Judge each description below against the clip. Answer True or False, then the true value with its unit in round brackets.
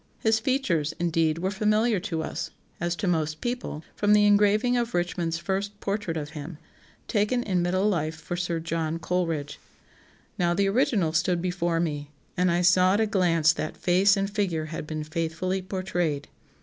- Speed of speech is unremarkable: True (175 wpm)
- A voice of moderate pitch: True (175 Hz)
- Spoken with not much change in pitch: False (3.8 semitones)